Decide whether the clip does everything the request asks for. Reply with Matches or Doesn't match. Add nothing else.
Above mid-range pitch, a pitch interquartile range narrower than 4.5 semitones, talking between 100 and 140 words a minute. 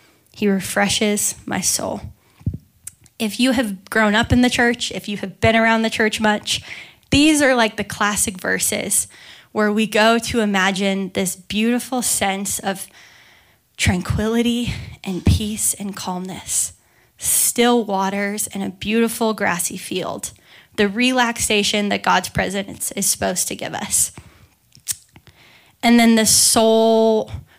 Matches